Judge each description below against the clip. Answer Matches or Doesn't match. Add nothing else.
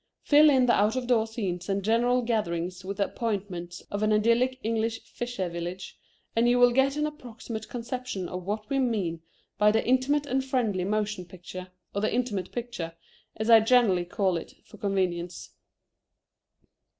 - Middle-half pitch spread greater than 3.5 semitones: Matches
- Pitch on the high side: Matches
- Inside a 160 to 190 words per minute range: Matches